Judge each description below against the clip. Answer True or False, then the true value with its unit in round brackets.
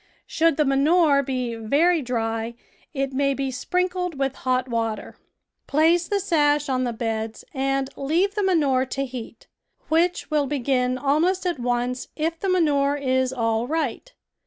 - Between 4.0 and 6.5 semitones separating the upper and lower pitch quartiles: True (4.4 semitones)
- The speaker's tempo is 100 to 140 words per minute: False (155 wpm)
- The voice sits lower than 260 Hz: False (275 Hz)